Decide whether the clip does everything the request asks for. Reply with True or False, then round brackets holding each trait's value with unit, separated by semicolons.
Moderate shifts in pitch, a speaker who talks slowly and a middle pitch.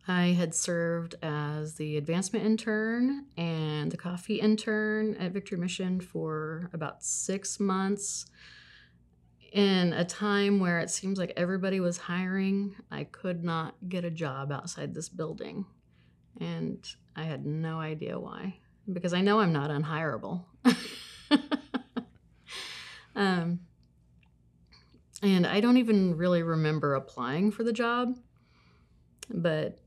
True (4.6 semitones; 125 wpm; 175 Hz)